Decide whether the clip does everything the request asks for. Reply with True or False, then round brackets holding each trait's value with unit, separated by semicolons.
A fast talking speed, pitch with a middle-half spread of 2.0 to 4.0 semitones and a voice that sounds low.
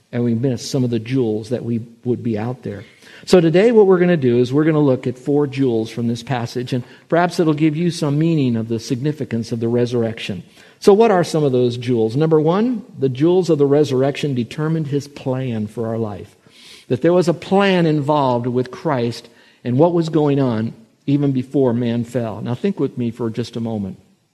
False (220 wpm; 5.0 semitones; 130 Hz)